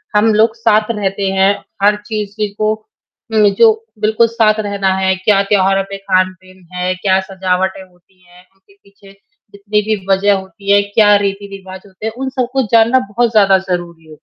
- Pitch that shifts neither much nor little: No, narrow, 2.1 semitones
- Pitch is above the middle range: Yes, high, 200 Hz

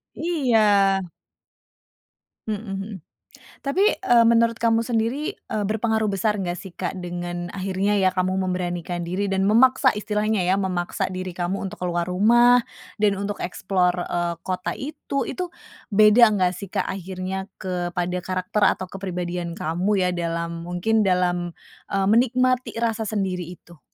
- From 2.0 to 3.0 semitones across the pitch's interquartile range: No, average, 3.6 semitones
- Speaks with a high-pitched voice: Yes, high, 195 Hz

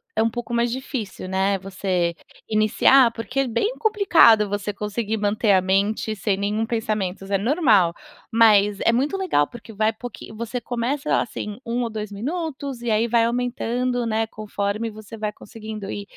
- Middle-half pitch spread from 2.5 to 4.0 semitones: Yes, average, 2.8 semitones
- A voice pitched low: No, high, 220 Hz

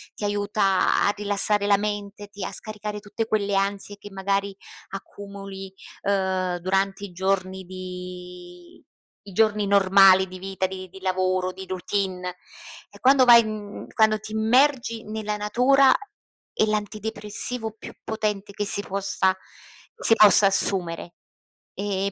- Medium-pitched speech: No, high, 200 Hz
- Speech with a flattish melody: Yes, narrow, 2.0 semitones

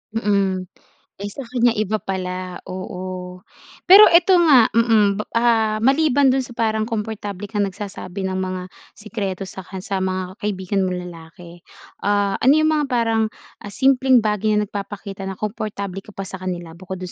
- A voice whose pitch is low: No, high, 205 Hz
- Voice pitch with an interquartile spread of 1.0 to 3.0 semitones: No, average, 3.4 semitones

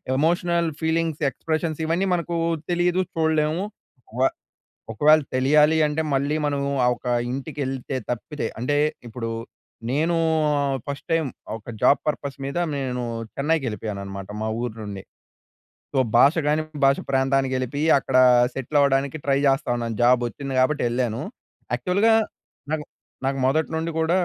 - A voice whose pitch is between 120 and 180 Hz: Yes, medium, 140 Hz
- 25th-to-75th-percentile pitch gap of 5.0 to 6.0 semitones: No, average, 3.6 semitones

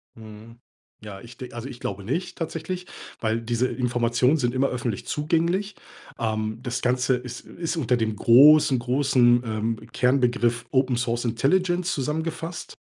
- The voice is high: No, low, 125 Hz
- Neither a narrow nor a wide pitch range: Yes, average, 4.3 semitones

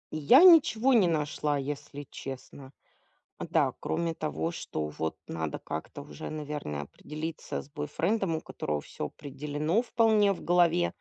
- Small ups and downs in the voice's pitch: No, average, 5.0 semitones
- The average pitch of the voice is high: No, medium, 150 Hz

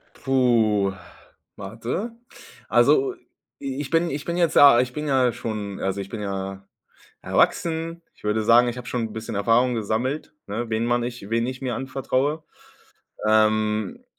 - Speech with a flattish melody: No, average, 3.8 semitones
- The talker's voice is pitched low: Yes, low, 120 Hz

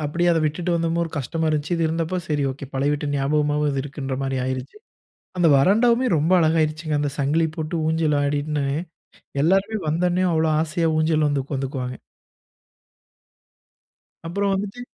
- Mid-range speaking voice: Yes, medium, 155 Hz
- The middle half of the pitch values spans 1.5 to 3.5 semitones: Yes, narrow, 2.6 semitones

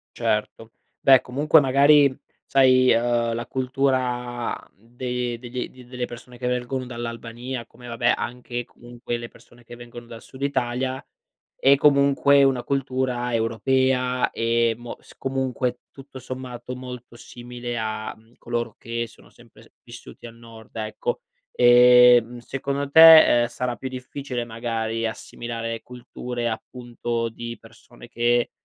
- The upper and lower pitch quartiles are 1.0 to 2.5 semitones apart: Yes, narrow, 1.6 semitones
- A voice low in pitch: Yes, low, 120 Hz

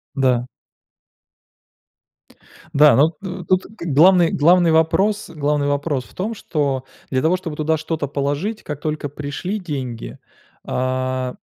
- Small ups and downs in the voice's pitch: No, average, 4.0 semitones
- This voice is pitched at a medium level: Yes, medium, 150 Hz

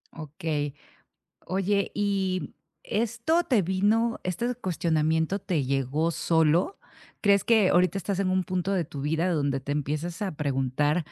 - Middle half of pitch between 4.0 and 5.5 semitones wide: Yes, average, 4.8 semitones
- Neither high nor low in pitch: Yes, medium, 175 Hz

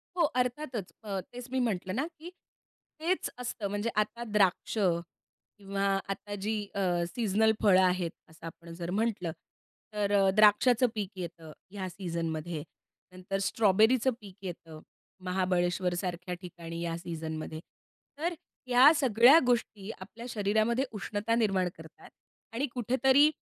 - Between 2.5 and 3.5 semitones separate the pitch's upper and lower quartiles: No, average, 4.8 semitones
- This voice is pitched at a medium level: No, high, 200 Hz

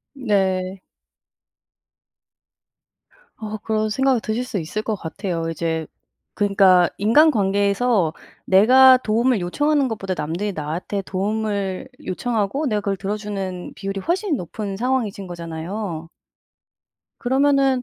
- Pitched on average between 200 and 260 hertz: Yes, high, 205 Hz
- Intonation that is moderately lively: Yes, average, 4.6 semitones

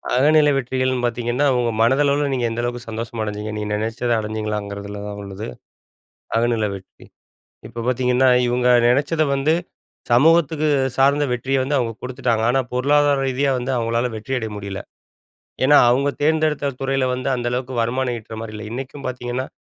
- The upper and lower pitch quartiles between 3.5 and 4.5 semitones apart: No, average, 3.1 semitones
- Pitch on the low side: Yes, low, 125 Hz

